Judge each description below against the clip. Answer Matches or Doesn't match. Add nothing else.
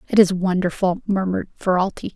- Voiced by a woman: Matches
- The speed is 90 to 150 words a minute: Matches